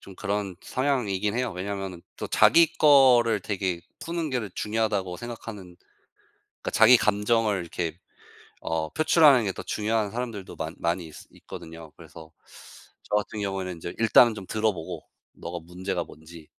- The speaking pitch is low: Yes, low, 100 Hz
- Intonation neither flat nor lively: Yes, average, 4.5 semitones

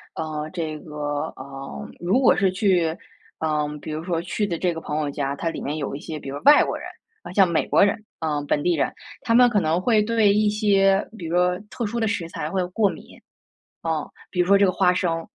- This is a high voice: No, medium, 175 Hz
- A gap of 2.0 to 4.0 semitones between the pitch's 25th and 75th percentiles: No, average, 4.5 semitones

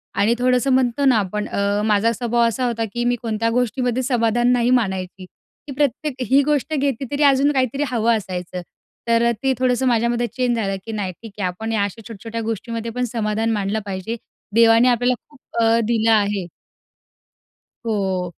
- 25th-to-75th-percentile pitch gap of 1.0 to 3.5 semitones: Yes, average, 2.9 semitones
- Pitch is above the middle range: Yes, high, 230 Hz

